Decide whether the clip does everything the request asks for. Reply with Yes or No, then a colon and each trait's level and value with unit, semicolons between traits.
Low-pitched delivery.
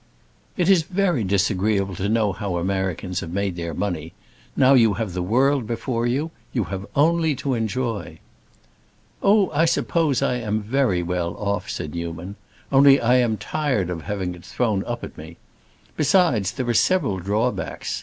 Yes: low, 110 Hz